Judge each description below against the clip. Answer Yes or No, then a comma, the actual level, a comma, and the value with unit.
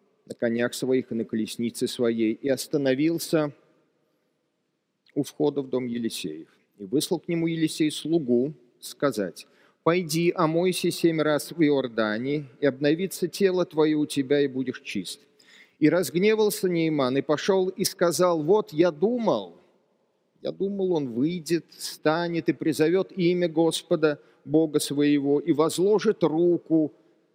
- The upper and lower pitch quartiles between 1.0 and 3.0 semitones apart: No, average, 3.7 semitones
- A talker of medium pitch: Yes, medium, 155 Hz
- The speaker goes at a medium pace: Yes, average, 130 wpm